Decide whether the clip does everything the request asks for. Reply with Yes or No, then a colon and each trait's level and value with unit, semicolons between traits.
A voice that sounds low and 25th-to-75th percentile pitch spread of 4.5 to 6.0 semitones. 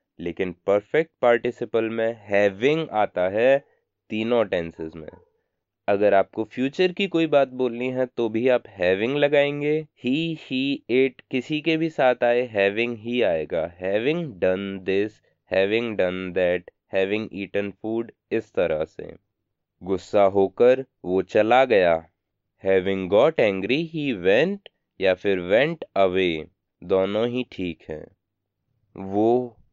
Yes: low, 110 Hz; average, 4.8 semitones